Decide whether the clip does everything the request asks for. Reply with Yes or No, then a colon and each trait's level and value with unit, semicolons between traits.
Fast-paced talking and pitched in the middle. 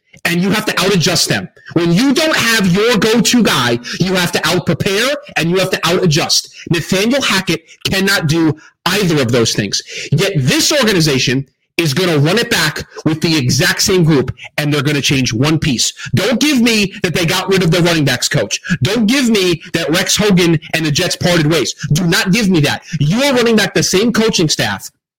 Yes: fast, 215 wpm; medium, 175 Hz